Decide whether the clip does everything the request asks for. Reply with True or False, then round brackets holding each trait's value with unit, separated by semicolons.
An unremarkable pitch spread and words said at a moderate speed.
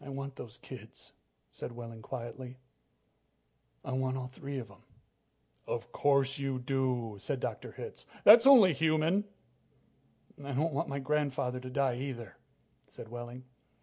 False (2.3 semitones; 145 wpm)